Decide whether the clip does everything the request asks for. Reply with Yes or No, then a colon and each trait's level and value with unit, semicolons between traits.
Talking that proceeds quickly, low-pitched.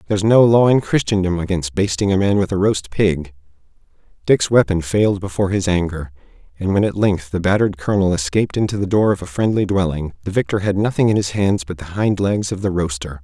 Yes: fast, 220 wpm; very low, 95 Hz